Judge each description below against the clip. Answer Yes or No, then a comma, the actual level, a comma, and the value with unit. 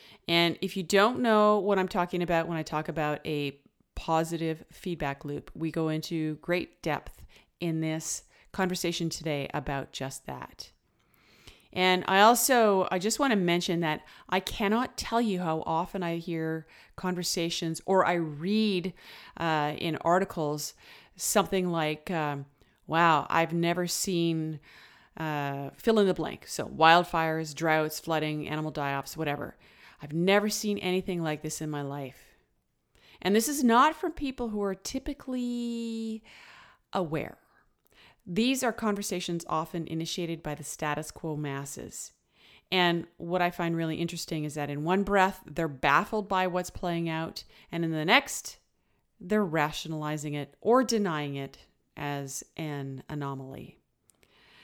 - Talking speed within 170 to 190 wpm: No, average, 145 wpm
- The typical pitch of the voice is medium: Yes, medium, 165 Hz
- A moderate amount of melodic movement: Yes, average, 3.8 semitones